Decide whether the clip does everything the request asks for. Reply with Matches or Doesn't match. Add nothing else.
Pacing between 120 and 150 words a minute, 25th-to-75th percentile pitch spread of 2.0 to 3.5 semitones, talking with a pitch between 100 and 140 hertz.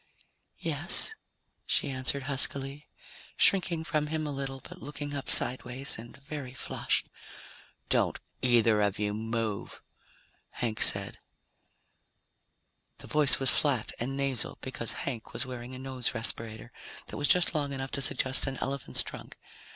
Matches